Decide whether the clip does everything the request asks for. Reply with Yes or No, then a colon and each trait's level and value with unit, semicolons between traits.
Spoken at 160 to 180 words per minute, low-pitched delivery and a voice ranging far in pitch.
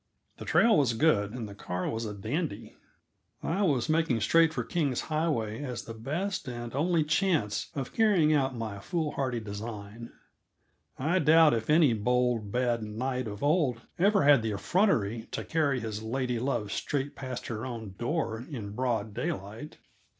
Yes: average, 165 wpm; low, 125 Hz; wide, 5.7 semitones